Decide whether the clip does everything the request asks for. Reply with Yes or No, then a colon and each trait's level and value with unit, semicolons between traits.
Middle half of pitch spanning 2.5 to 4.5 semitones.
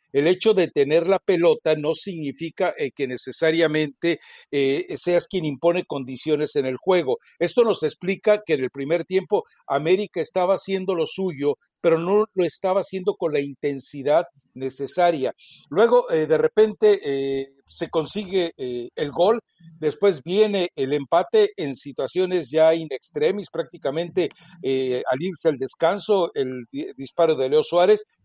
No: average, 5.0 semitones